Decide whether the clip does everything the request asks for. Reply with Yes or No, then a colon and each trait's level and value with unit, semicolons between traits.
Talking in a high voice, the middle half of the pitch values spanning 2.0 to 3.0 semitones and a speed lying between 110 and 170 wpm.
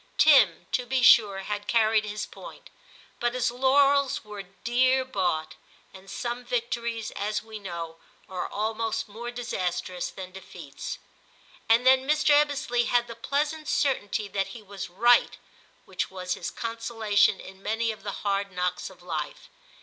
No: high, 220 Hz; average, 4.2 semitones; average, 150 wpm